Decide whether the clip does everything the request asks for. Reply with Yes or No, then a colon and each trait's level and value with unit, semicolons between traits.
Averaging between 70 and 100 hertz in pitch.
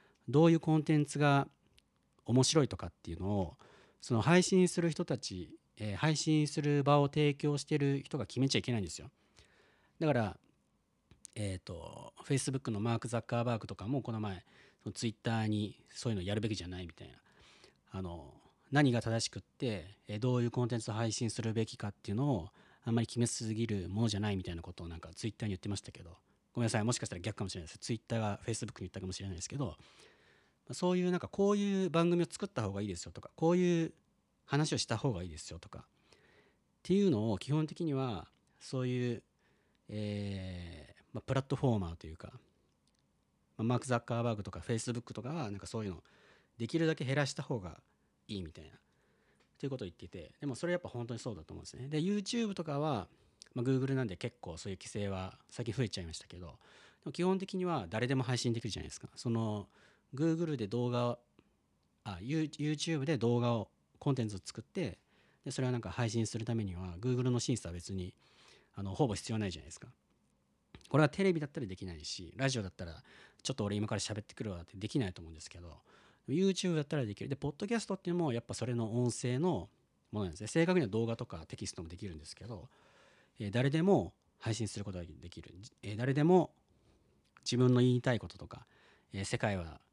No: low, 115 Hz